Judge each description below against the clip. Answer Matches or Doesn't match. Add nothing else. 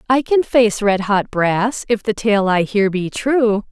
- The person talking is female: Matches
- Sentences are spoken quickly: Matches